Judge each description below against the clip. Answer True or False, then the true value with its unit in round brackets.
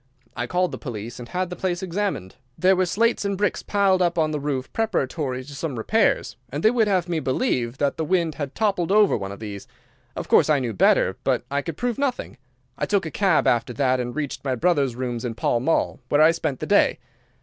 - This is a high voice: False (155 Hz)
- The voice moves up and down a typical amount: False (6.6 semitones)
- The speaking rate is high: True (230 wpm)